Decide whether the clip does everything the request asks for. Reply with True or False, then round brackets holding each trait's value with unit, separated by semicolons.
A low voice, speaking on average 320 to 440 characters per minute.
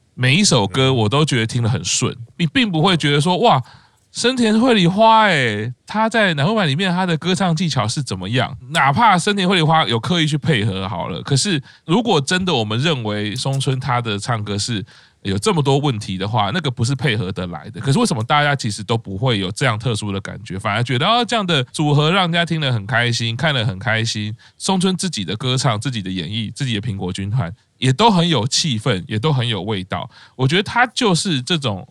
True (130 Hz; 330 characters per minute)